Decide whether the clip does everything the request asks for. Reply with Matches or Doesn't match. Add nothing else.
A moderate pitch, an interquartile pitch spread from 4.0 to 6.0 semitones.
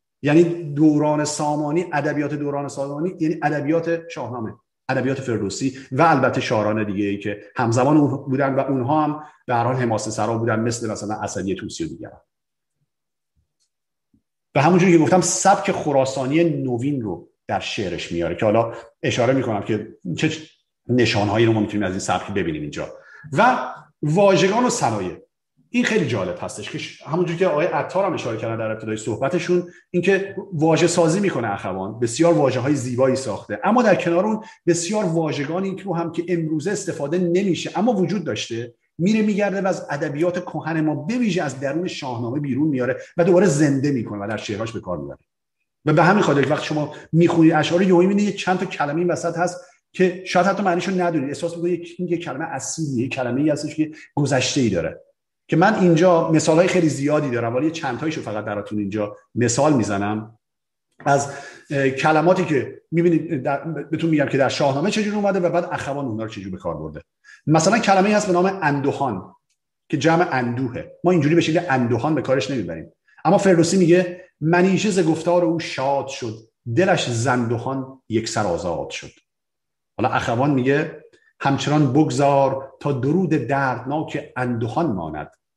Matches